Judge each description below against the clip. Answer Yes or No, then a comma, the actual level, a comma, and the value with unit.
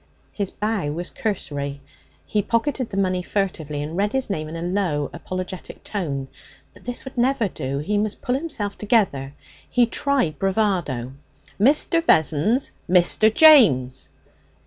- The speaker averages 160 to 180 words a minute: No, average, 145 wpm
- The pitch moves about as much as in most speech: No, wide, 6.6 semitones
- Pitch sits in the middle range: No, high, 195 Hz